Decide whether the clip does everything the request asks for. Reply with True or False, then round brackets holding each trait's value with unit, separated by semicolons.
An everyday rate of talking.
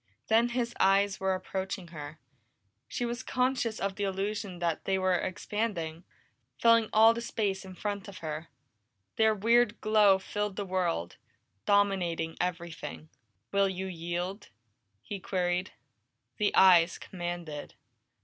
False (130 wpm)